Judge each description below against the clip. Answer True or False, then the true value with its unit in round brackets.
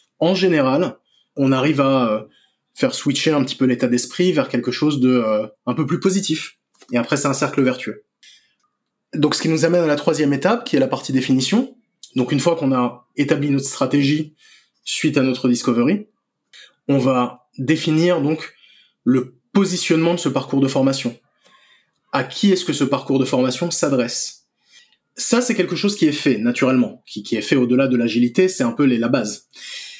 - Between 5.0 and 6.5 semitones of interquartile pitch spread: True (5.3 semitones)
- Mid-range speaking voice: True (145 Hz)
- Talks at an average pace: True (185 wpm)